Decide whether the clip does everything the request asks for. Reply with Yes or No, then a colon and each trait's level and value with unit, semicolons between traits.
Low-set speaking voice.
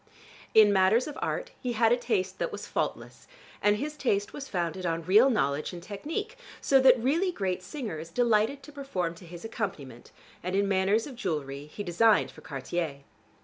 No: high, 205 Hz